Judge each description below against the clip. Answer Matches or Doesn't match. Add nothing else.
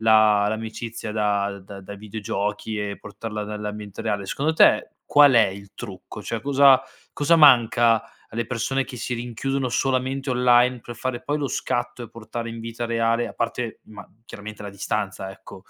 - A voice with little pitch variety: Doesn't match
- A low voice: Matches